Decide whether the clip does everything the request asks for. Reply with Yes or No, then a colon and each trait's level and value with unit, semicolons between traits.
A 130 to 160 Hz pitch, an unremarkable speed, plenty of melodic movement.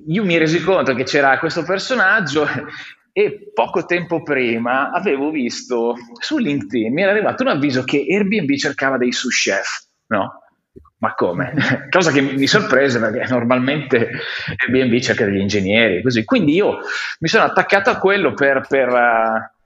Yes: medium, 140 Hz; average, 155 wpm; wide, 7.5 semitones